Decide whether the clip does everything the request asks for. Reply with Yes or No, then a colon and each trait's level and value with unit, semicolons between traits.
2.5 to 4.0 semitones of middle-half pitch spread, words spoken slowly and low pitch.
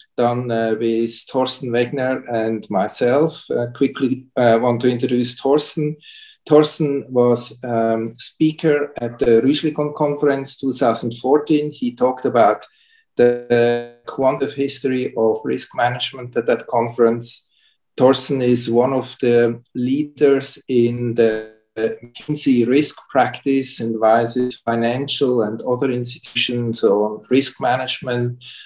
Yes: average, 2.8 semitones; slow, 115 wpm; low, 125 Hz